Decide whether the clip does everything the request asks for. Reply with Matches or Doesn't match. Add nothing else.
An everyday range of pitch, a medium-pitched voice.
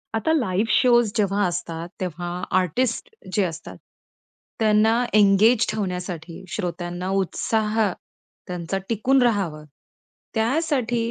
Doesn't match